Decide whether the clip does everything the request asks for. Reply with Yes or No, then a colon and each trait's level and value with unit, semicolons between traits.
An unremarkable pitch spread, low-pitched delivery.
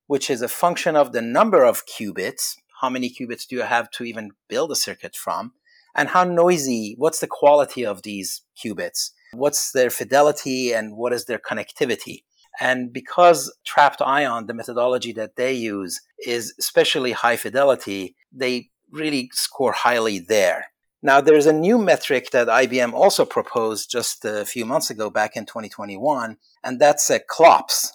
Yes: average, 4.9 semitones; low, 125 Hz